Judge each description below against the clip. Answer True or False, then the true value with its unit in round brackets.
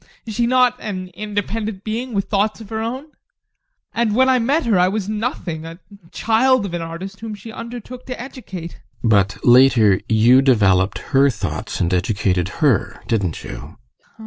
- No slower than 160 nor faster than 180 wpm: True (170 wpm)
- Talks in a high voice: True (195 Hz)